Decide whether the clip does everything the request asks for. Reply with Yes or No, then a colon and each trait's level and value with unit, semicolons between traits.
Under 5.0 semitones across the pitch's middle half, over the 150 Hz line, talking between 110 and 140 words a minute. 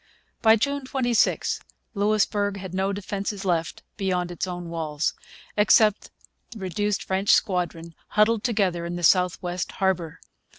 Yes: average, 2.9 semitones; high, 190 Hz; slow, 135 wpm